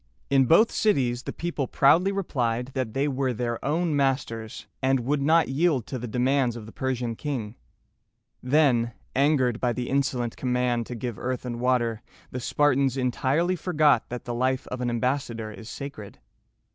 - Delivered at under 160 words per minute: No, average, 170 wpm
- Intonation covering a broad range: No, average, 2.7 semitones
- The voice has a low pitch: Yes, low, 130 Hz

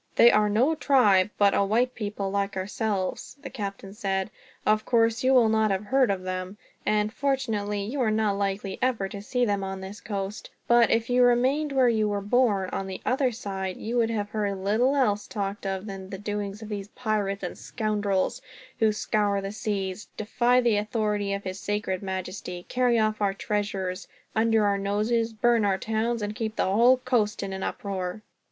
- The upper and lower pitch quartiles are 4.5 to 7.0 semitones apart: No, narrow, 2.6 semitones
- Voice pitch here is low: No, high, 210 Hz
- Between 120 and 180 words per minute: No, average, 195 wpm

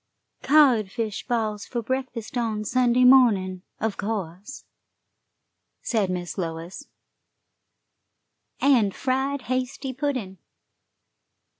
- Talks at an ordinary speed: No, slow, 85 wpm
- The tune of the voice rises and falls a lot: No, average, 4.6 semitones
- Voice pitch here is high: Yes, high, 230 Hz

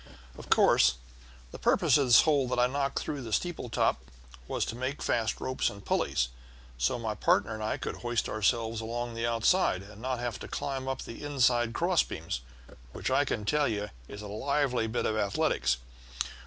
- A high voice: No, low, 115 Hz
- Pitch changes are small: No, average, 3.6 semitones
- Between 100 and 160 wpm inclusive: No, average, 195 wpm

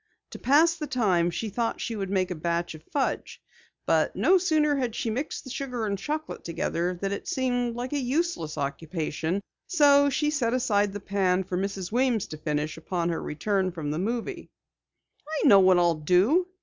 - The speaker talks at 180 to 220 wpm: Yes, average, 190 wpm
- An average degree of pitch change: No, wide, 7.2 semitones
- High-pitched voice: Yes, high, 205 Hz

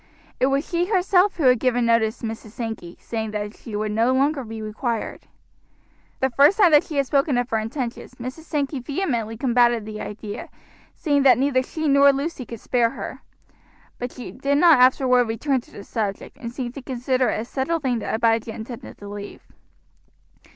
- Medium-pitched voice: No, very high, 250 Hz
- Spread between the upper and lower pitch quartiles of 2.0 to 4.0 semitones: Yes, average, 3.7 semitones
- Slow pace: No, average, 195 wpm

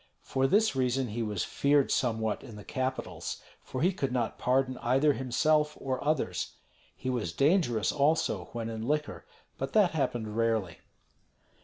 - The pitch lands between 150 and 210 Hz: No, low, 130 Hz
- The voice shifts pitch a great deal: No, average, 4.6 semitones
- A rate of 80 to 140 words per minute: No, average, 155 wpm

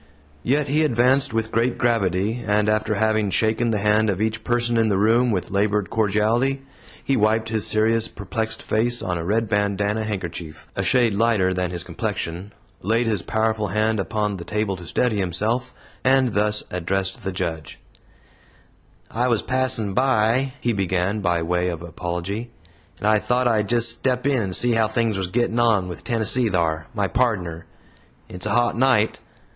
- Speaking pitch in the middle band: No, low, 110 Hz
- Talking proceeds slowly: No, average, 175 wpm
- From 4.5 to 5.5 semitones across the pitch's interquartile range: No, average, 3.5 semitones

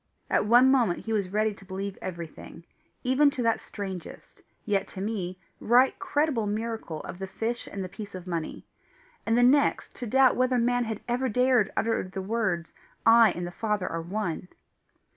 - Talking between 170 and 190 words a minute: Yes, average, 180 wpm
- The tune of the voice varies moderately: Yes, average, 4.5 semitones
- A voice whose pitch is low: No, high, 215 Hz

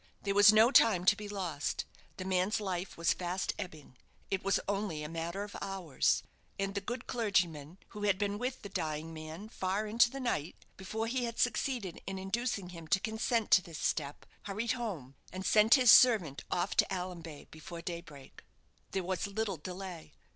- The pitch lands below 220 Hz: Yes, high, 190 Hz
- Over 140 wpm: Yes, average, 185 wpm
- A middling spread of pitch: Yes, average, 4.0 semitones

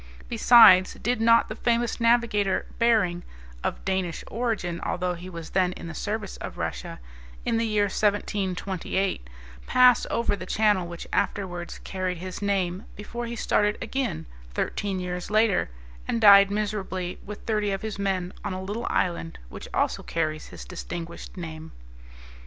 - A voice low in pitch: No, high, 195 Hz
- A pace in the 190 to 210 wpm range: No, average, 150 wpm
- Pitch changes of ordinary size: Yes, average, 3.4 semitones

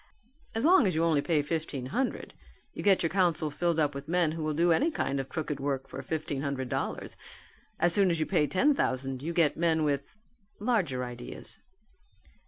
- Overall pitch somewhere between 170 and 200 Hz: No, medium, 155 Hz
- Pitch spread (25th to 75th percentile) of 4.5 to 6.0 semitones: No, average, 3.8 semitones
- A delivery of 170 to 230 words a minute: Yes, average, 195 wpm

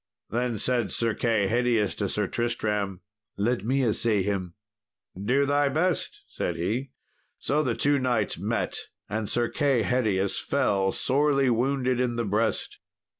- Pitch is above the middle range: No, low, 120 Hz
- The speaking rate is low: No, average, 145 wpm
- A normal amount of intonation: Yes, average, 3.9 semitones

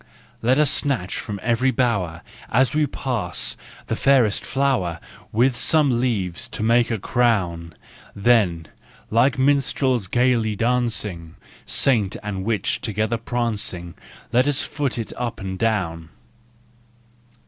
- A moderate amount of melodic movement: Yes, average, 4.5 semitones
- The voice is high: No, low, 115 Hz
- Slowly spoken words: Yes, slow, 125 wpm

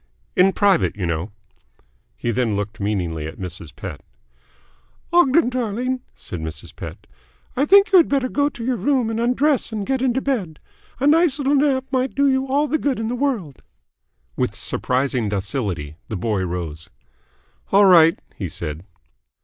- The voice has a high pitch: Yes, high, 215 Hz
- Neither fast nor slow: Yes, average, 165 wpm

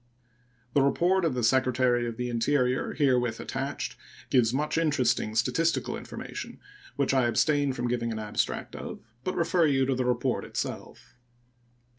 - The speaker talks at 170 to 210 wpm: No, average, 150 wpm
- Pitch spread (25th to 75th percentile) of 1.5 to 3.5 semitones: Yes, average, 3.2 semitones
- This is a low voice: Yes, low, 130 Hz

